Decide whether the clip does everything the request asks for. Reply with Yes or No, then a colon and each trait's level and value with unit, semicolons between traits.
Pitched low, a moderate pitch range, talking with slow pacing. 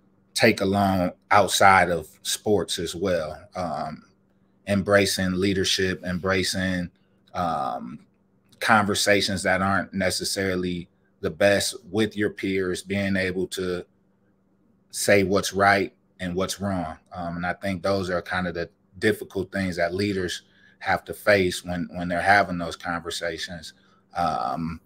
No: very low, 95 Hz; narrow, 1.5 semitones; slow, 130 wpm